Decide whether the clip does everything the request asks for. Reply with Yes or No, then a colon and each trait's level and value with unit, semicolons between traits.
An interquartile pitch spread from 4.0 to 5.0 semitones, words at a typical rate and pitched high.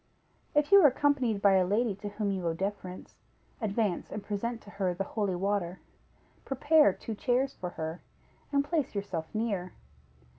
Yes: average, 4.6 semitones; average, 170 wpm; high, 205 Hz